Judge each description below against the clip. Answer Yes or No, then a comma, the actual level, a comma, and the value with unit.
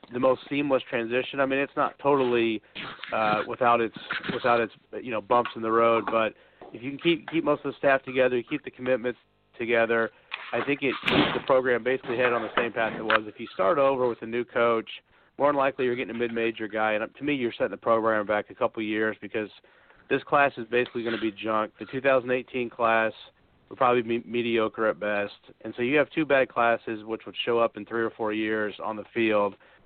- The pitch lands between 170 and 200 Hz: No, low, 120 Hz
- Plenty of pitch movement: No, average, 2.7 semitones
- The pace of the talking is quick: Yes, fast, 235 wpm